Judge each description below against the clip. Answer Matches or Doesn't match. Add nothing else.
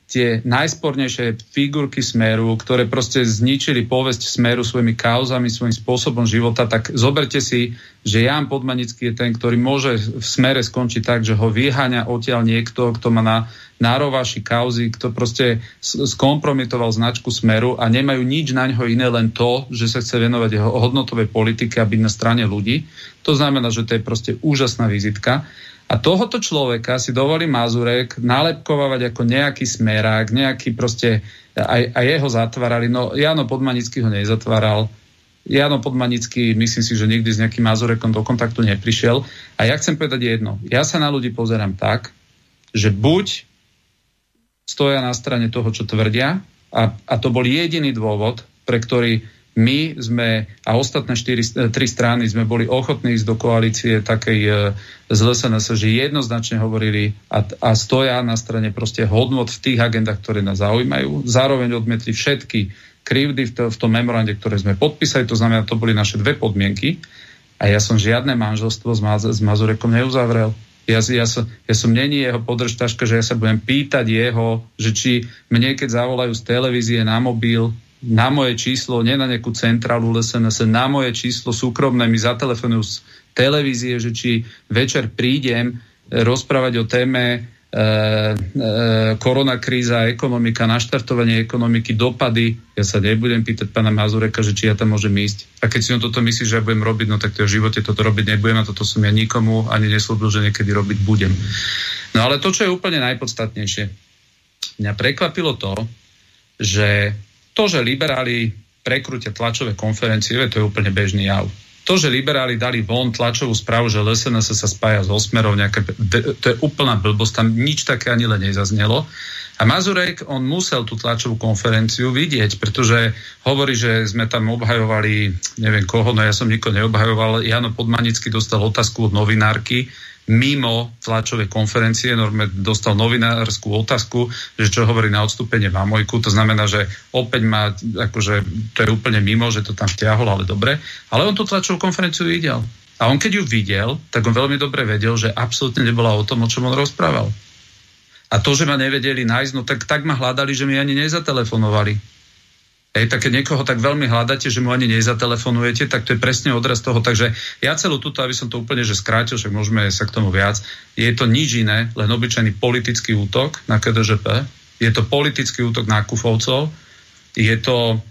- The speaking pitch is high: Doesn't match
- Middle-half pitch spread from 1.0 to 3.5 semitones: Matches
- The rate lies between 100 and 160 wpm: Doesn't match